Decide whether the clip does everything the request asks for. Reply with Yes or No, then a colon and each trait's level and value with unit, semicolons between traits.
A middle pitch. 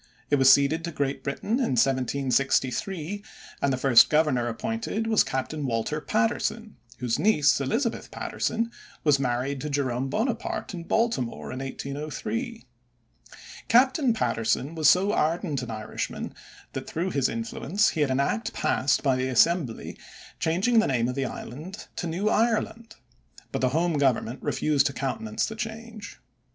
Yes: medium, 150 Hz